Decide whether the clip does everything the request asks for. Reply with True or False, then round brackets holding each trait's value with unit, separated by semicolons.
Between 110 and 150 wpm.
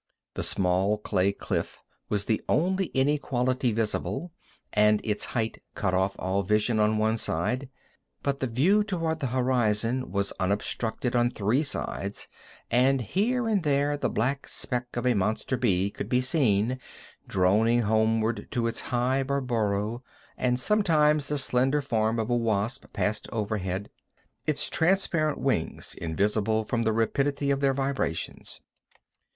True (145 wpm)